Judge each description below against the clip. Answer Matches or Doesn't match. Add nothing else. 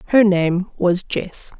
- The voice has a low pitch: Doesn't match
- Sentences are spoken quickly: Doesn't match